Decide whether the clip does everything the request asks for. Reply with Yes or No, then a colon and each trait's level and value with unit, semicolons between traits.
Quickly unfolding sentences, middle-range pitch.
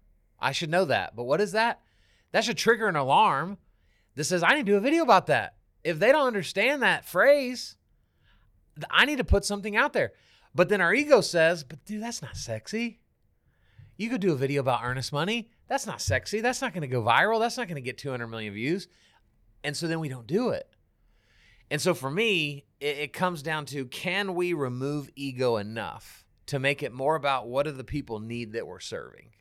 Yes: fast, 215 wpm; medium, 150 Hz